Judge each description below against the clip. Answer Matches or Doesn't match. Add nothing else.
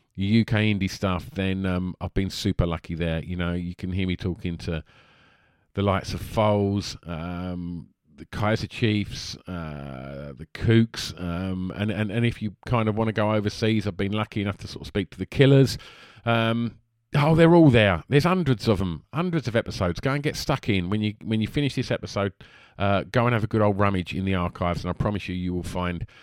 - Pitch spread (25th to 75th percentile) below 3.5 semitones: Doesn't match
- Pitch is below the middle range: Matches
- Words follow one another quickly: Matches